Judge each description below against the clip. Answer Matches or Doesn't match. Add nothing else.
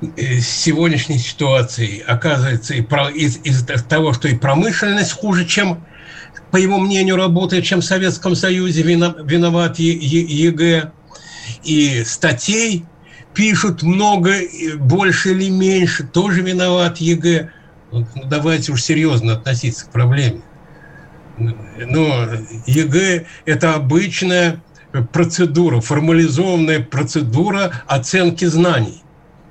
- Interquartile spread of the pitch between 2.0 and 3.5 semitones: Doesn't match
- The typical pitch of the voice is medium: Matches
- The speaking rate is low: Matches